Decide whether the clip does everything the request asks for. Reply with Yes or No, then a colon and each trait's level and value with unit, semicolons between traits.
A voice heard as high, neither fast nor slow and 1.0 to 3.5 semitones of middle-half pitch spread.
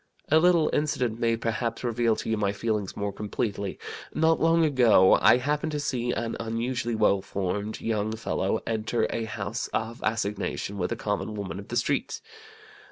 No: low, 115 Hz; average, 170 wpm; average, 3.0 semitones